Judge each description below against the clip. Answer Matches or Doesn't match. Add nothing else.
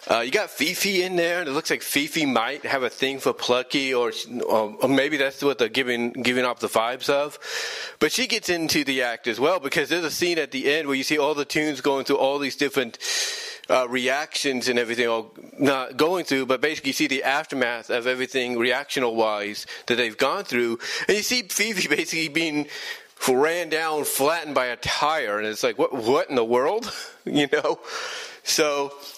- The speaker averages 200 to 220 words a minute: Matches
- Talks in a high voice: Doesn't match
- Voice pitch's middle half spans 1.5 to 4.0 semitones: Doesn't match